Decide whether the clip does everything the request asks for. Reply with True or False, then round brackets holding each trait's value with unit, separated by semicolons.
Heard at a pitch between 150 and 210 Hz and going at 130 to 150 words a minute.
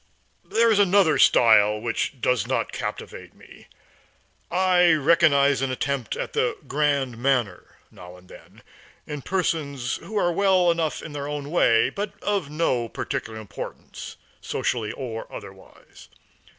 False (140 Hz; 135 wpm)